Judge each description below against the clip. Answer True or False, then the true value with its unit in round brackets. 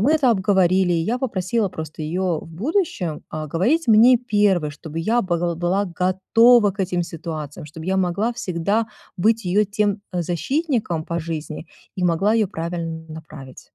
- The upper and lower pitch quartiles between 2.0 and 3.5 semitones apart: False (4.5 semitones)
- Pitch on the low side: False (185 Hz)